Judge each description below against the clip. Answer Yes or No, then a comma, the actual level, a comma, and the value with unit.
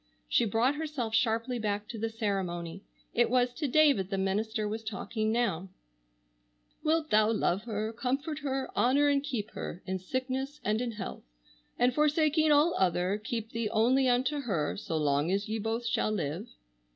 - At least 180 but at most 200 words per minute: No, average, 170 wpm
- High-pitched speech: Yes, high, 225 Hz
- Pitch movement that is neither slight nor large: Yes, average, 4.4 semitones